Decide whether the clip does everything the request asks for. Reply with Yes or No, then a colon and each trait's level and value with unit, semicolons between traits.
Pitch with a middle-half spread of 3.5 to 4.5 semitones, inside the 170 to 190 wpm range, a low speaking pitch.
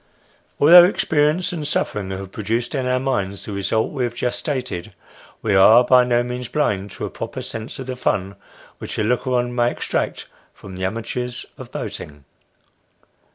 Yes: average, 4.2 semitones; average, 175 wpm; low, 120 Hz